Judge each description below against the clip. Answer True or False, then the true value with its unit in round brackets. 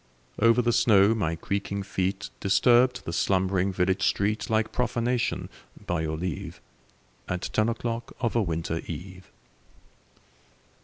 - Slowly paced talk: True (125 wpm)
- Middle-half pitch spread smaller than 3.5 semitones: False (4.1 semitones)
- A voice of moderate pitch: False (100 Hz)